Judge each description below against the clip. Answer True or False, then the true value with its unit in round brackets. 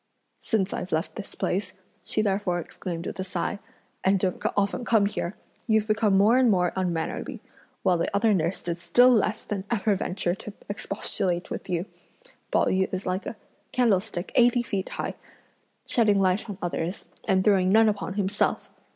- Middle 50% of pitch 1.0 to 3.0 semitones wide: True (2.6 semitones)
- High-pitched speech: True (195 Hz)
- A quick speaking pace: False (170 wpm)